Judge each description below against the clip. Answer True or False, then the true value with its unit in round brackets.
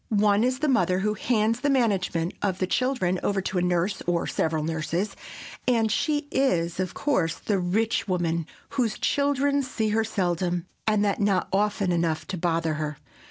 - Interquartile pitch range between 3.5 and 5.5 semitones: True (4.4 semitones)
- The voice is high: True (195 Hz)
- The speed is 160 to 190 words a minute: True (175 wpm)